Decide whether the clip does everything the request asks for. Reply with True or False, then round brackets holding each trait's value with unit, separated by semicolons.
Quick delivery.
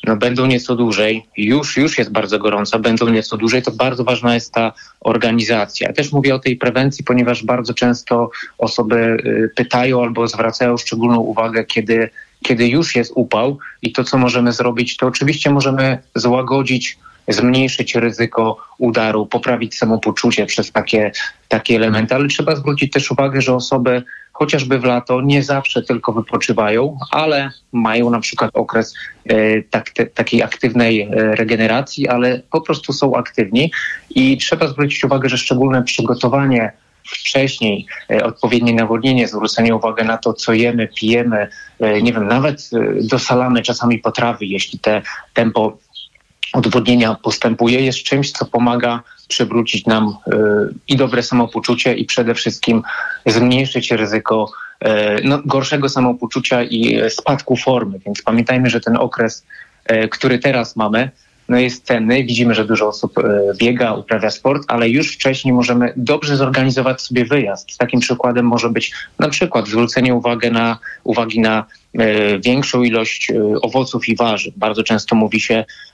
False (145 wpm)